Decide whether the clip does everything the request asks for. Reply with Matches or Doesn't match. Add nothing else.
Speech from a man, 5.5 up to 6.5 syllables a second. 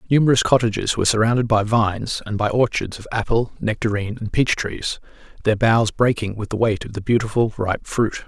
Matches